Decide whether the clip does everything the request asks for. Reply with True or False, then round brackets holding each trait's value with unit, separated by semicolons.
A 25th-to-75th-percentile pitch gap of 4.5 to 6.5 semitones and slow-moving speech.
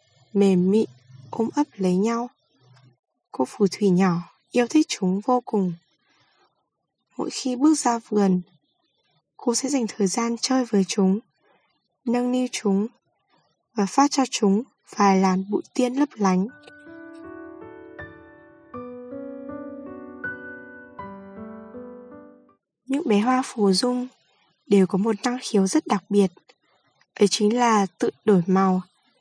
True (5.2 semitones; 125 wpm)